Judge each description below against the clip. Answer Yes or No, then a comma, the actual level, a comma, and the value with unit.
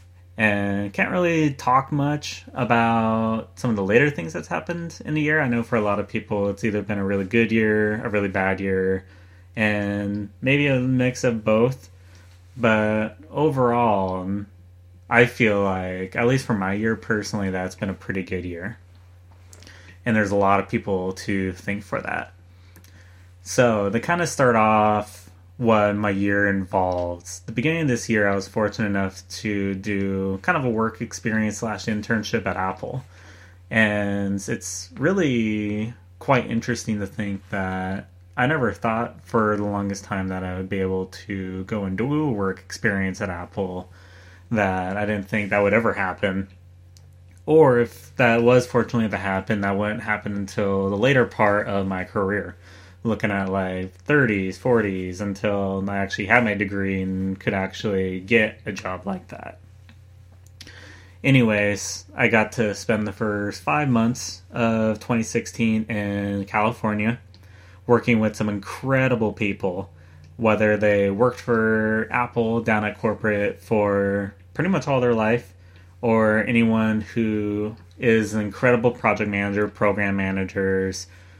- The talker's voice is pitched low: Yes, low, 100 Hz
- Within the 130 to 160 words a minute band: Yes, average, 155 wpm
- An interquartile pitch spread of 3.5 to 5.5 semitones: No, average, 3.0 semitones